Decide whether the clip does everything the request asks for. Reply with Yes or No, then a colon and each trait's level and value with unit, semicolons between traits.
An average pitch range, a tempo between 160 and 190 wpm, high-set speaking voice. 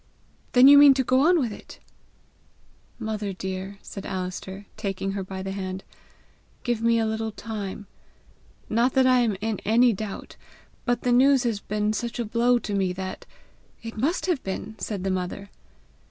Yes: average, 3.9 semitones; average, 180 wpm; high, 220 Hz